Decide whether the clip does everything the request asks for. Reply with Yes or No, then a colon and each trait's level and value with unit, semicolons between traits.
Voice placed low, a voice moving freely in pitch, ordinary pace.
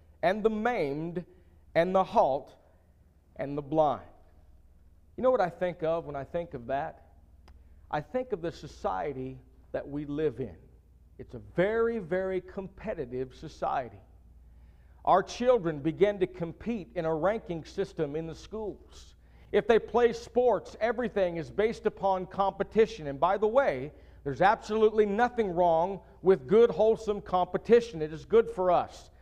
No: medium, 170 Hz; wide, 8.1 semitones; average, 150 wpm